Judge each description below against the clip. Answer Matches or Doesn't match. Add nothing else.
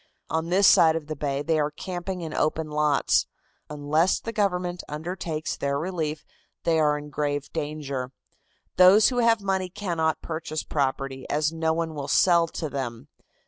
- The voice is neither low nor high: Matches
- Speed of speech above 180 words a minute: Doesn't match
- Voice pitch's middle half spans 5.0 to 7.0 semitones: Doesn't match